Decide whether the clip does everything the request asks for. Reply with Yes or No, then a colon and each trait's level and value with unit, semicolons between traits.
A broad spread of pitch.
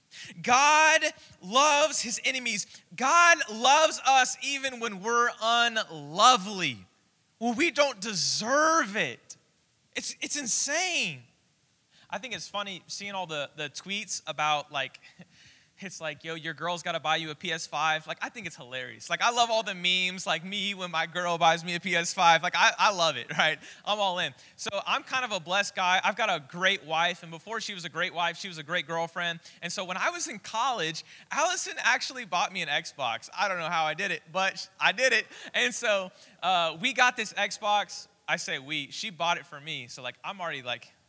Yes: wide, 6.4 semitones